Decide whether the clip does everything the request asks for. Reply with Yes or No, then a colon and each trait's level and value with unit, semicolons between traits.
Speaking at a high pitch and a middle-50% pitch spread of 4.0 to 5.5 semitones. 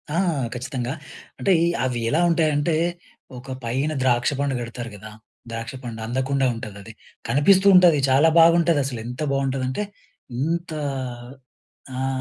No: low, 135 Hz; average, 4.3 semitones